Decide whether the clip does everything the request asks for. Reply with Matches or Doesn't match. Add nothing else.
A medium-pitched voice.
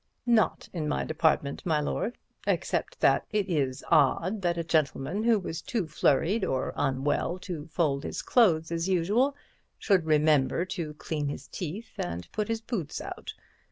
Matches